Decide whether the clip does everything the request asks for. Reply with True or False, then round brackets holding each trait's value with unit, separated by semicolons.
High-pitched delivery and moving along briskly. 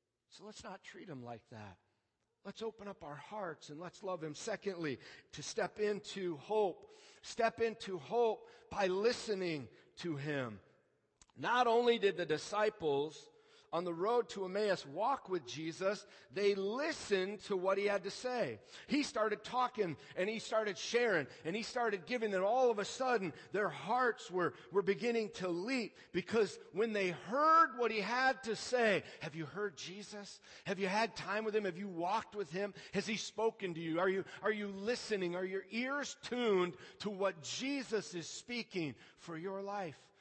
False (200 Hz; 175 wpm)